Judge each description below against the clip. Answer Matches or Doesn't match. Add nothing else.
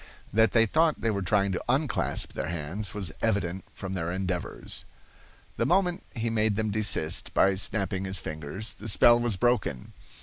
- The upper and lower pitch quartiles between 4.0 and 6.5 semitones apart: Doesn't match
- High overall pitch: Doesn't match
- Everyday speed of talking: Matches